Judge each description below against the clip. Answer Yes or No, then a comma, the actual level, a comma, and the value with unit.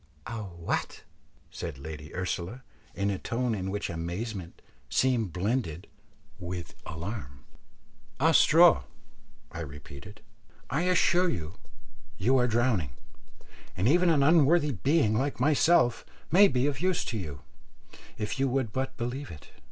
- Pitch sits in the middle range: No, low, 110 Hz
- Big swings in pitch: Yes, wide, 7.7 semitones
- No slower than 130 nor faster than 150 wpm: Yes, slow, 135 wpm